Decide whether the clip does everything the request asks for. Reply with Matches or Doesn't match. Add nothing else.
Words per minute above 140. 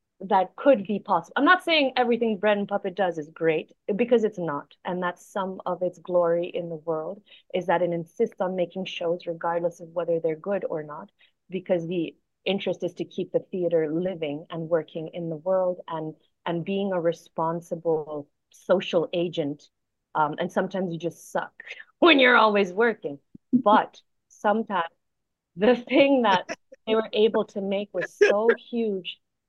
Matches